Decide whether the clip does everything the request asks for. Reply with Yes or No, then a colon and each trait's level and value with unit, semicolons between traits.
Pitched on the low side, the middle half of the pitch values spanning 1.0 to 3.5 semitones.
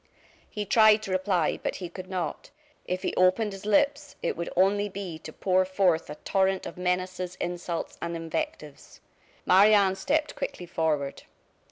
No: medium, 185 Hz; average, 2.7 semitones